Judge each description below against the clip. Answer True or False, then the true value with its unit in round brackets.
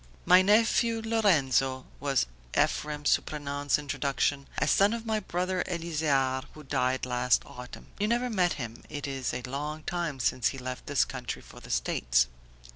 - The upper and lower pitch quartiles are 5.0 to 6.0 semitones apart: True (5.6 semitones)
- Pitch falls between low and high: True (145 Hz)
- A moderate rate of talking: True (160 wpm)